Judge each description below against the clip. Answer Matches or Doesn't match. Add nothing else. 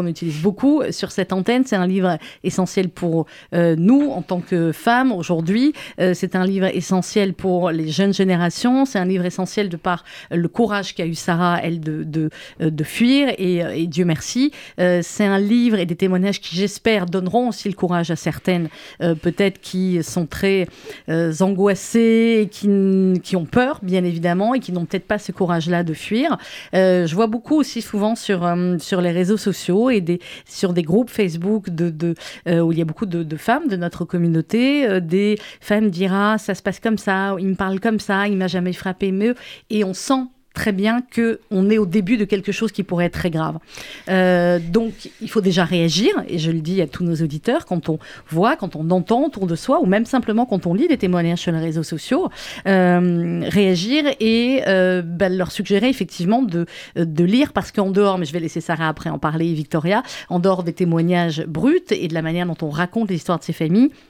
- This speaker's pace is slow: Doesn't match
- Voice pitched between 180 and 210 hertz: Matches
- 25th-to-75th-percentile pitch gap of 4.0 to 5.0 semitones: Doesn't match